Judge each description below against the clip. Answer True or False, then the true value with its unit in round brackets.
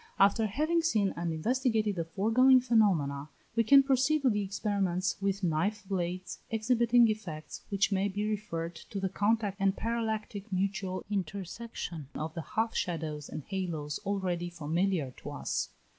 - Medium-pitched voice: False (195 Hz)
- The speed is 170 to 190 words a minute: False (150 wpm)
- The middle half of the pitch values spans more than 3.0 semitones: True (4.2 semitones)